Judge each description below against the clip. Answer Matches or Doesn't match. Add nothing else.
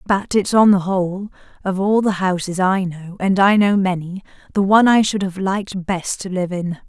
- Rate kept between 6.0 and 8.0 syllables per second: Doesn't match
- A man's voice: Doesn't match